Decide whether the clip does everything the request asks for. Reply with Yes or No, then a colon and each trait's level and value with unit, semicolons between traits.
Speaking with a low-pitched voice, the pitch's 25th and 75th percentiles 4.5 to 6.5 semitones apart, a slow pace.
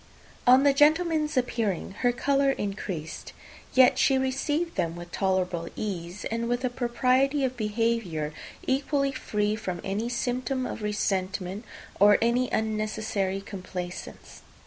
No: high, 225 Hz; average, 5.1 semitones; slow, 125 wpm